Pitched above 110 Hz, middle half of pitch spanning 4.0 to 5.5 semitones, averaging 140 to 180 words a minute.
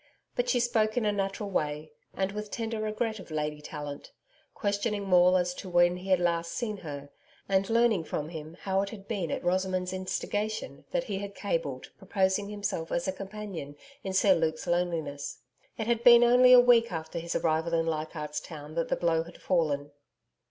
No: medium, 185 Hz; average, 4.4 semitones; average, 190 wpm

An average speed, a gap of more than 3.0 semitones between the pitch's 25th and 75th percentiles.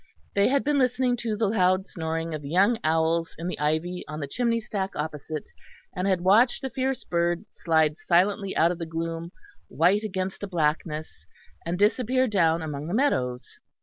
Yes: average, 180 wpm; average, 4.7 semitones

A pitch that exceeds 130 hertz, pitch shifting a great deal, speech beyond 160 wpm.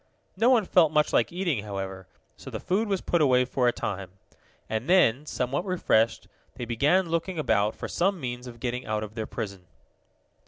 No: low, 125 Hz; wide, 8.0 semitones; average, 190 wpm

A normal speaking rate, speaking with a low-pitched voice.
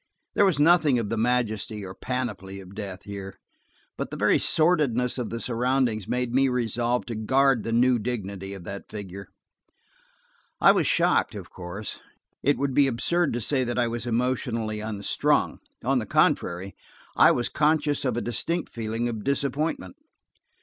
Yes: average, 165 wpm; low, 120 Hz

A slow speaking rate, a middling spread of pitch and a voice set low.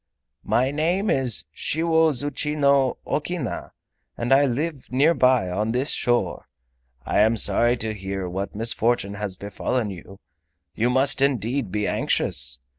Yes: slow, 130 wpm; average, 5.0 semitones; low, 125 Hz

